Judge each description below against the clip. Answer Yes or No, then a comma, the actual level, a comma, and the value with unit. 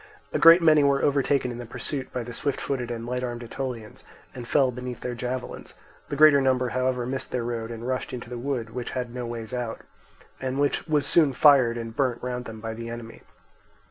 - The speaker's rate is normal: No, fast, 215 wpm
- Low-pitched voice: Yes, low, 125 Hz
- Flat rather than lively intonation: Yes, narrow, 2.2 semitones